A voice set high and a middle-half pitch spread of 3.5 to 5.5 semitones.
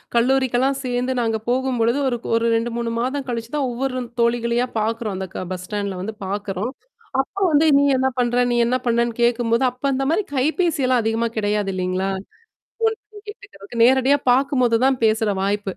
No: high, 240 Hz; average, 2.8 semitones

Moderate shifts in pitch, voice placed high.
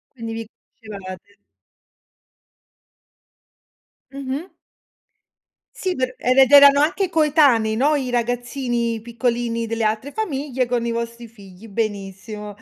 Yes: average, 3.4 semitones; high, 235 Hz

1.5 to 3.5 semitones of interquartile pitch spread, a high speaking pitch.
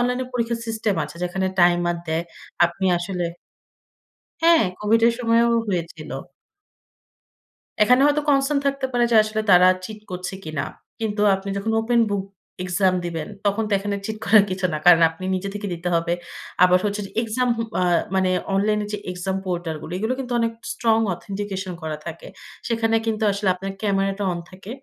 No: average, 3.9 semitones; high, 200 Hz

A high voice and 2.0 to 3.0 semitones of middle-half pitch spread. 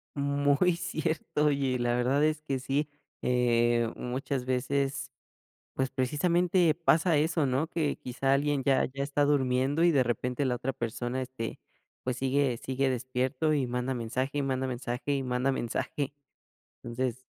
No: low, 135 Hz; narrow, 2.5 semitones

